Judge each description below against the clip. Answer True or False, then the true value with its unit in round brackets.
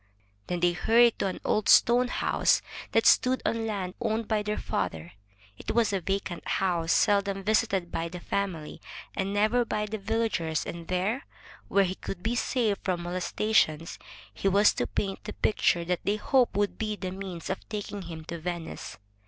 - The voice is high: True (195 Hz)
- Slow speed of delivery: False (185 wpm)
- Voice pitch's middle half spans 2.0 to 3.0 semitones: False (3.5 semitones)